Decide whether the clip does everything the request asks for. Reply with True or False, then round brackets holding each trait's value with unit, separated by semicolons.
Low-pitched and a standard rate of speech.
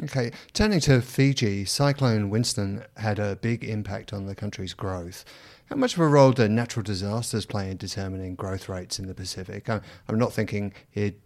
True (105 Hz; 180 wpm)